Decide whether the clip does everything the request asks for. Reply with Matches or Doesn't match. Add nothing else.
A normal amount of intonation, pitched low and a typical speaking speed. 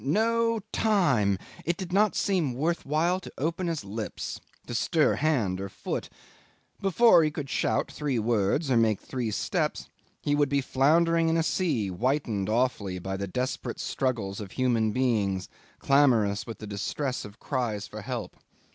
Doesn't match